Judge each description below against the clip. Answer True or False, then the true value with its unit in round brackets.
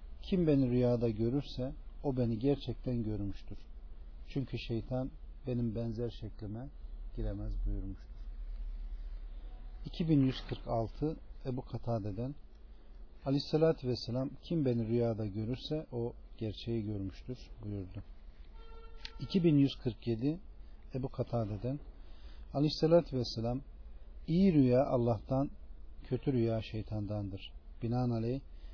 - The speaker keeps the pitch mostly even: False (4.8 semitones)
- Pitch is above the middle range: False (115 Hz)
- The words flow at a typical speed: False (90 wpm)